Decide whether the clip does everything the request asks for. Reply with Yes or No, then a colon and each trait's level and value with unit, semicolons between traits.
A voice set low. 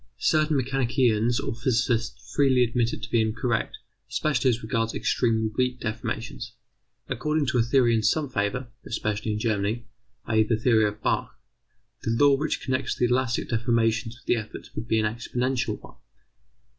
Yes: low, 115 Hz